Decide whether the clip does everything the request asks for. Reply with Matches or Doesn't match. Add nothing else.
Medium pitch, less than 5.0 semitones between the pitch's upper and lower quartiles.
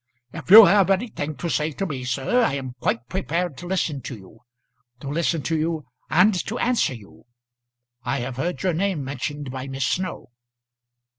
Doesn't match